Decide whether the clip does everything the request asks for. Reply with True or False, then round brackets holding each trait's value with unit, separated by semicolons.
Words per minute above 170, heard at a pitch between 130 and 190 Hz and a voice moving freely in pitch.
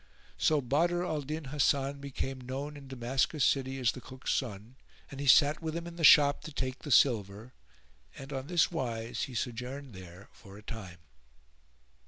False (180 wpm; 135 Hz; 3.4 semitones)